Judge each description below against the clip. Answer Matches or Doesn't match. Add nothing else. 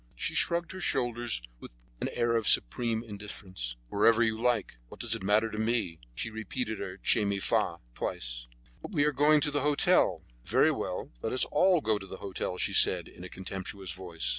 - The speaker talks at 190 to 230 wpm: Matches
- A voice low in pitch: Matches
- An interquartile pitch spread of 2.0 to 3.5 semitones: Doesn't match